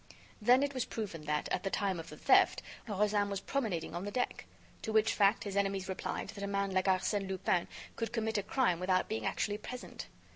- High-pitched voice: Yes, high, 200 Hz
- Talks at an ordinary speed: No, fast, 215 wpm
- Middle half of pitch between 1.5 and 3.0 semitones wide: Yes, average, 2.7 semitones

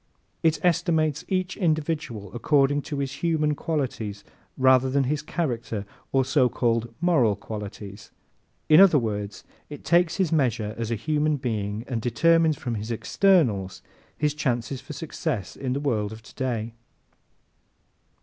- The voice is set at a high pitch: No, low, 135 Hz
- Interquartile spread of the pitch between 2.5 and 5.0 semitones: No, wide, 5.5 semitones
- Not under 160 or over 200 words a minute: No, average, 140 wpm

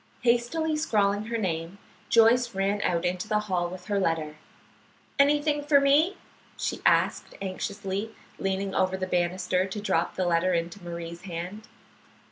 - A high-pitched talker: Yes, high, 195 Hz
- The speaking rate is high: No, average, 145 wpm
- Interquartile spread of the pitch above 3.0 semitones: Yes, average, 4.3 semitones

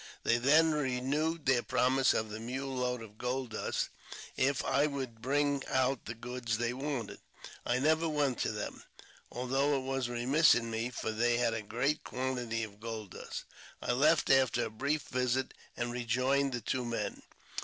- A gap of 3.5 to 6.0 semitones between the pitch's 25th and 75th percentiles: No, average, 2.7 semitones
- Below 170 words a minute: No, average, 175 wpm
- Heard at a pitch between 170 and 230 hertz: No, low, 125 Hz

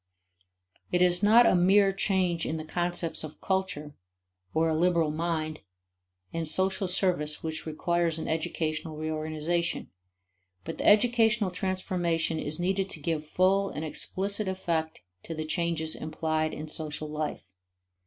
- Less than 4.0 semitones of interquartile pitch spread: Yes, average, 3.1 semitones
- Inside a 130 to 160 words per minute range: Yes, average, 140 wpm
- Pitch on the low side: No, medium, 170 Hz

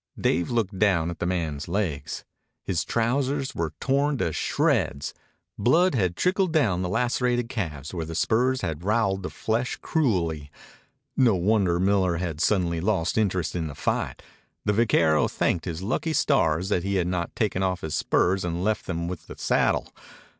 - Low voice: Yes, very low, 95 Hz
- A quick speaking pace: No, average, 170 wpm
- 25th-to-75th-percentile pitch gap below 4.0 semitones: No, average, 5.3 semitones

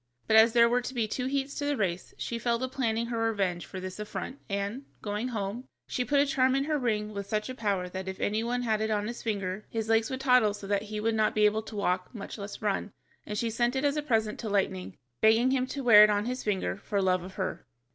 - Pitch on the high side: Yes, high, 220 Hz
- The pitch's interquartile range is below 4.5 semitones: Yes, average, 3.4 semitones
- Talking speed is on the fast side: Yes, fast, 270 wpm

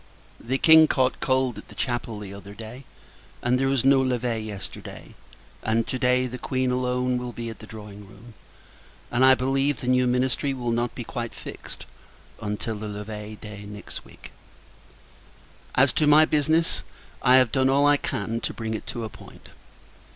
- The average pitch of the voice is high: No, low, 125 Hz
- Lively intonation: No, average, 3.1 semitones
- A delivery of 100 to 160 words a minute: No, average, 180 wpm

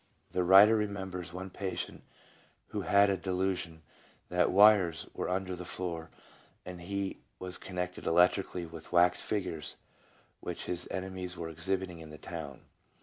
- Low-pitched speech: Yes, very low, 90 Hz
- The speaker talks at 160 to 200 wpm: No, average, 145 wpm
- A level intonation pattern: Yes, narrow, 1.6 semitones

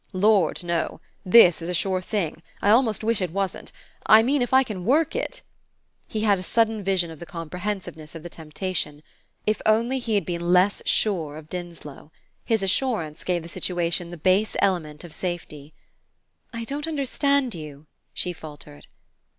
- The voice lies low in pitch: No, medium, 185 Hz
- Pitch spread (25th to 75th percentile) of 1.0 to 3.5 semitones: No, average, 4.8 semitones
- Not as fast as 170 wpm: No, average, 175 wpm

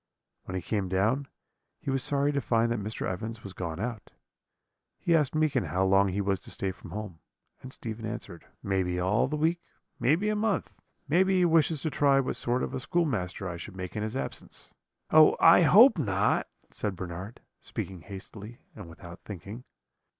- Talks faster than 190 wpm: No, average, 185 wpm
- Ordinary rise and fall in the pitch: No, wide, 7.2 semitones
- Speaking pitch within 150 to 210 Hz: No, low, 110 Hz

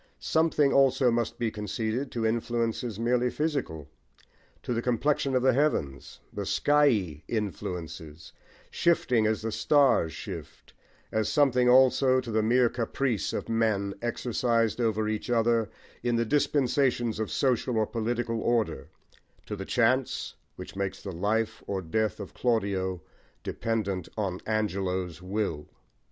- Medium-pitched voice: No, low, 115 Hz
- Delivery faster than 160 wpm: No, slow, 135 wpm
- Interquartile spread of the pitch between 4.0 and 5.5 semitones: No, average, 3.5 semitones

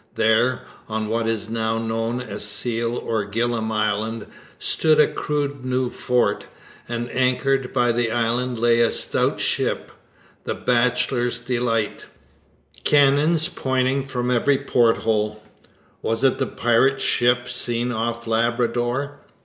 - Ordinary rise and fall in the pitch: No, narrow, 2.1 semitones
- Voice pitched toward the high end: No, low, 120 Hz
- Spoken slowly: Yes, slow, 125 wpm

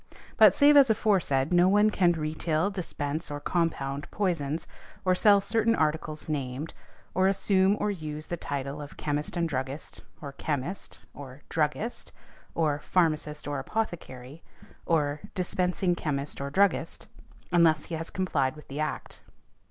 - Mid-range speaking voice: Yes, medium, 160 Hz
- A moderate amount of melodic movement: Yes, average, 4.3 semitones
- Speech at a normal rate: Yes, average, 145 wpm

